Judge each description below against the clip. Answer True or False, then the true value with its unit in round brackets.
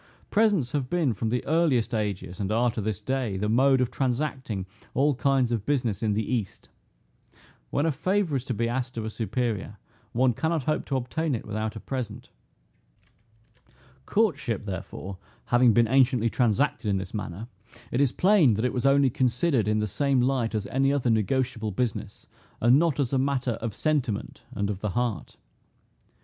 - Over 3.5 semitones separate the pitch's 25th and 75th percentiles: True (4.0 semitones)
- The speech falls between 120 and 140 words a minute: False (180 wpm)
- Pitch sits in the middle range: False (125 Hz)